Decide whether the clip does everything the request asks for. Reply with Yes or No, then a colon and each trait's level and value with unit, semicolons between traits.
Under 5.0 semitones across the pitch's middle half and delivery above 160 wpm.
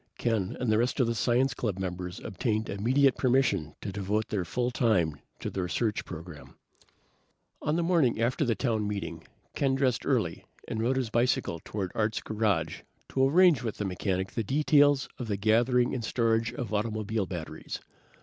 Yes: average, 4.2 semitones; average, 175 wpm